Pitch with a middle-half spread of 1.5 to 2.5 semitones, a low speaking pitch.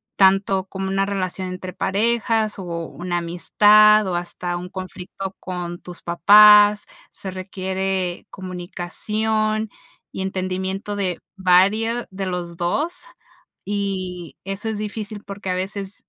No: narrow, 2.2 semitones; high, 190 Hz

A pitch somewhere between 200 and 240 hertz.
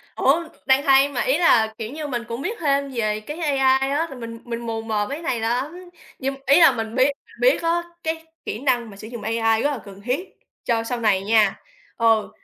No: very high, 250 Hz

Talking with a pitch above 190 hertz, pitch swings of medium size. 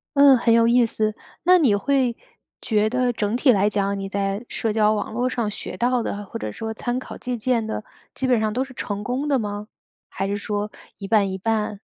Yes: high, 220 Hz; average, 3.3 semitones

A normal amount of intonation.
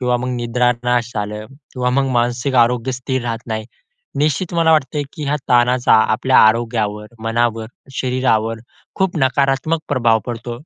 No: narrow, 2.3 semitones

